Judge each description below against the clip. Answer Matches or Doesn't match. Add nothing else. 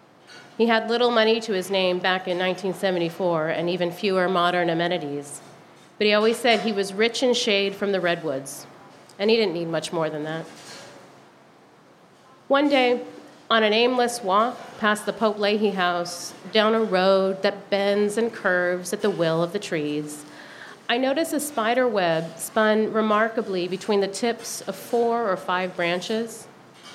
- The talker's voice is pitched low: Doesn't match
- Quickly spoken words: Doesn't match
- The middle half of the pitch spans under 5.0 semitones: Matches